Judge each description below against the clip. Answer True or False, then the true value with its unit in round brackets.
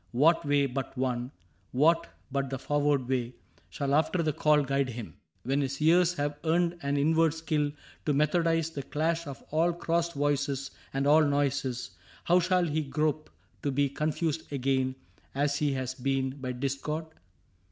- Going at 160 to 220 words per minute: True (165 wpm)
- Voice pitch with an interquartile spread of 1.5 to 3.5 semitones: True (2.8 semitones)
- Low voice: False (145 Hz)